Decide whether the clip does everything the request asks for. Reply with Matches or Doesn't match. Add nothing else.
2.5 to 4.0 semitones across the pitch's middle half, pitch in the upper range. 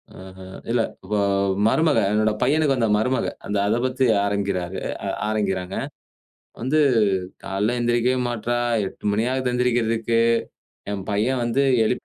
Doesn't match